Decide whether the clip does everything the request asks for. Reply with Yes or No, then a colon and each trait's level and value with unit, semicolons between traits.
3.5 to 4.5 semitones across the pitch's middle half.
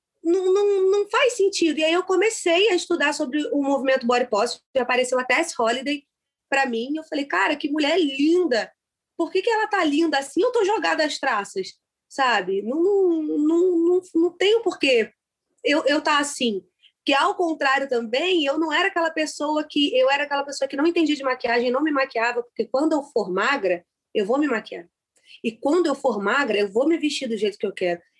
No: average, 4.9 semitones